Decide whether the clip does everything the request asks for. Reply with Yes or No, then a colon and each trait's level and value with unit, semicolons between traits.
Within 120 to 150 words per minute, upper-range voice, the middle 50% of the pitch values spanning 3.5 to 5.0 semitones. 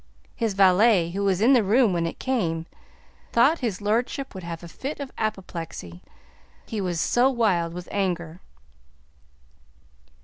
No: average, 145 wpm; high, 195 Hz; wide, 5.4 semitones